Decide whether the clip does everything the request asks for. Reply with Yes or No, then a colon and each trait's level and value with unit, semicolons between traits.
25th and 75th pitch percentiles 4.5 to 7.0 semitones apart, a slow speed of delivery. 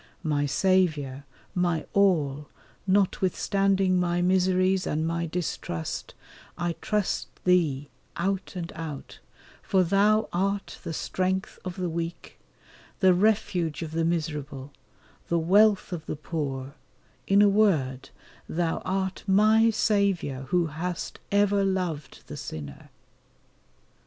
No: average, 3.7 semitones; slow, 115 wpm